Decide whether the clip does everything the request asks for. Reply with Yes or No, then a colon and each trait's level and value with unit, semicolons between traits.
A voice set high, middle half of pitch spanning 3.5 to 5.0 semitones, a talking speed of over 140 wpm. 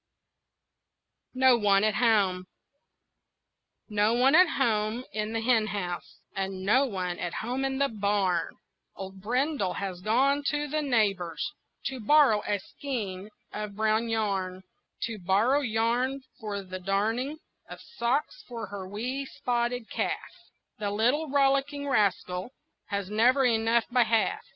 No: high, 220 Hz; average, 4.5 semitones; slow, 135 wpm